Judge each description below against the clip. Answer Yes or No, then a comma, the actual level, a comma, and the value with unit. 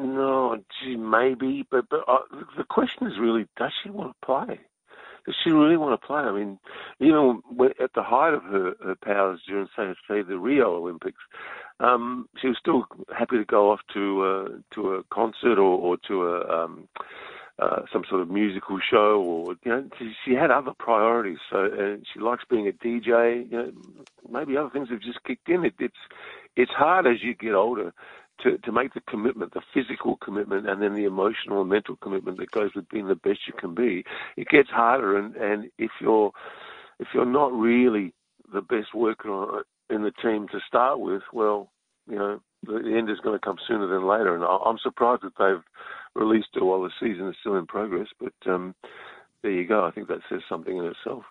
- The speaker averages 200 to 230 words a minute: Yes, fast, 205 wpm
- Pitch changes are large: No, average, 4.3 semitones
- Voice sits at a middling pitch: No, low, 115 Hz